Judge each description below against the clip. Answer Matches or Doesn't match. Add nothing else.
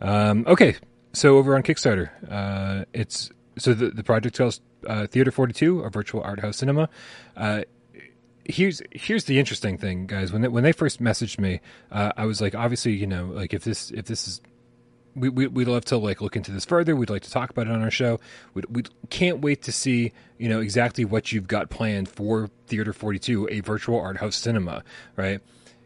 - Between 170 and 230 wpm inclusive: Matches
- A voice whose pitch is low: Matches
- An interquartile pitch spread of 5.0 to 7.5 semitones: Doesn't match